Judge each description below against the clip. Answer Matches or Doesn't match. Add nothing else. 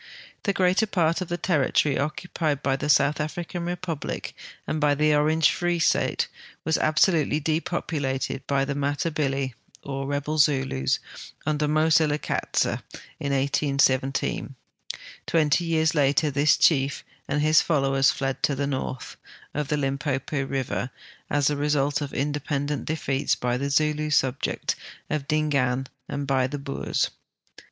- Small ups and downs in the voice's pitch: Matches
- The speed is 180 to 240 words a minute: Doesn't match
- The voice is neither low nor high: Matches